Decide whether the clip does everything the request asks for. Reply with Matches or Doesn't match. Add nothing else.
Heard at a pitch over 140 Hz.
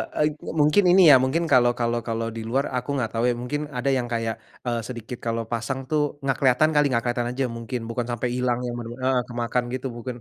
Doesn't match